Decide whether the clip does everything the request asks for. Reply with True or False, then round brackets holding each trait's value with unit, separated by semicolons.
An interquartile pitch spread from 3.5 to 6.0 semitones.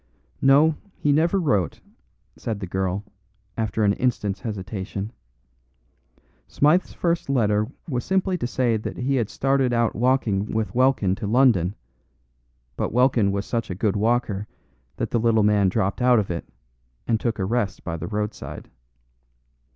True (4.1 semitones)